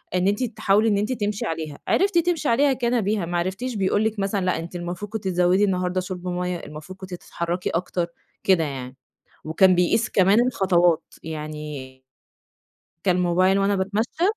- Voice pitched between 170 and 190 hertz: Yes, medium, 185 Hz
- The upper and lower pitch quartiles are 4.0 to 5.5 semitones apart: No, average, 3.2 semitones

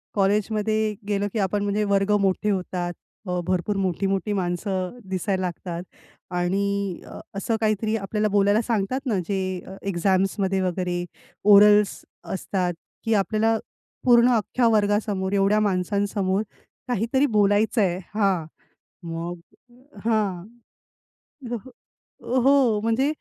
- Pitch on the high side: Yes, high, 200 Hz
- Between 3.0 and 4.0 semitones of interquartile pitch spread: No, narrow, 2.4 semitones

